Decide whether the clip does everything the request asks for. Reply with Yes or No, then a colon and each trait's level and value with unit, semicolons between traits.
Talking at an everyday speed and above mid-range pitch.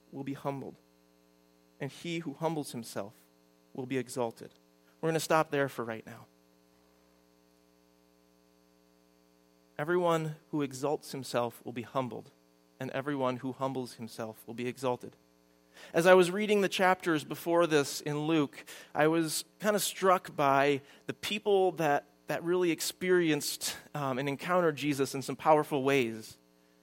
No: average, 145 wpm; low, 135 Hz